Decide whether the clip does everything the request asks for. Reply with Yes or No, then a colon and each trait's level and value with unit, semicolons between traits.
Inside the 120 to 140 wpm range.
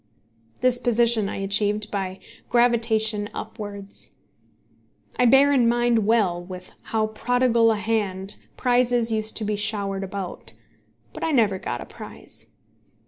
Yes: slow, 135 wpm